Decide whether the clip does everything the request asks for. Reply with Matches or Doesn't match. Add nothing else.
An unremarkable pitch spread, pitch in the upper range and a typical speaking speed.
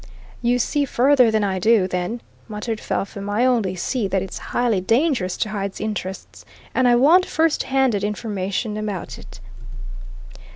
Matches